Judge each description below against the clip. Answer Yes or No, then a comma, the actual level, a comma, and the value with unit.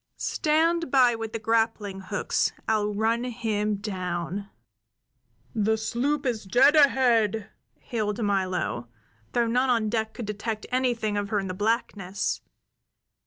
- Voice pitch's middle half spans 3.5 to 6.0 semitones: No, average, 2.9 semitones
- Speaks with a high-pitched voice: Yes, high, 220 Hz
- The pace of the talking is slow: Yes, slow, 130 wpm